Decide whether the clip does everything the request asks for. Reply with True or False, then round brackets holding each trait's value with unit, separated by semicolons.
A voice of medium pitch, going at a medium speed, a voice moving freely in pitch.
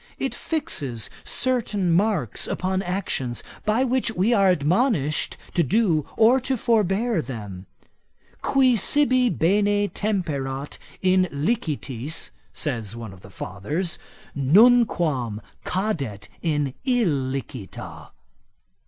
False (180 Hz; 100 wpm; 8.5 semitones)